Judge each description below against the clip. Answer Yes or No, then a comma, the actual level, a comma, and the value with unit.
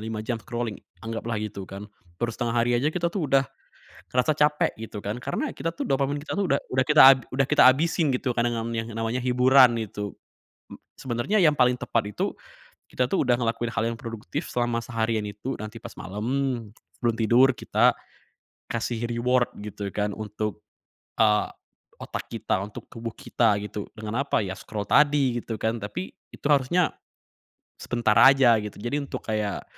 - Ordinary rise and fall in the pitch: Yes, average, 3.7 semitones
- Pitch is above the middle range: No, low, 120 Hz